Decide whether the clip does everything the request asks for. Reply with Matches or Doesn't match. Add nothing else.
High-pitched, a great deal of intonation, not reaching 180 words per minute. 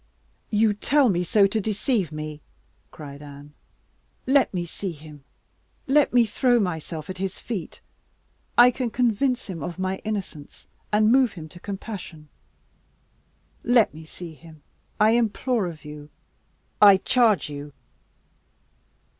Matches